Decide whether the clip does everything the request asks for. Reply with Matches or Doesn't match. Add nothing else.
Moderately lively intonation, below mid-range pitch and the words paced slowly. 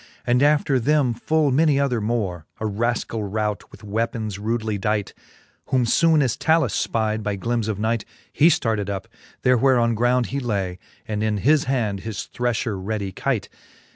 Doesn't match